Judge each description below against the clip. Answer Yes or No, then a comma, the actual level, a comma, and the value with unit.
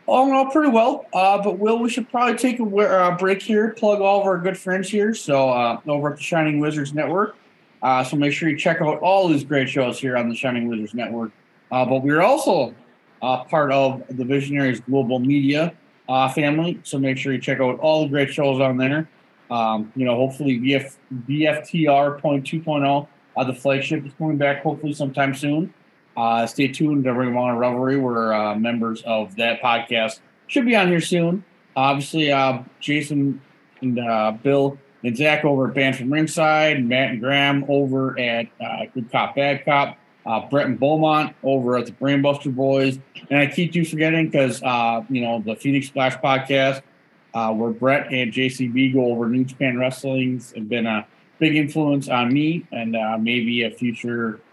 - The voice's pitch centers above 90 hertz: Yes, medium, 140 Hz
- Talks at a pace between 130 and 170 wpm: No, average, 195 wpm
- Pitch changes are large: No, average, 3.5 semitones